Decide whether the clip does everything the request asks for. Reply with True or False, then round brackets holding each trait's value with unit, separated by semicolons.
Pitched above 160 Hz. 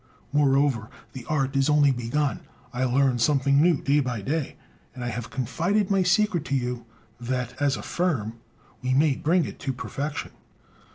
False (135 Hz)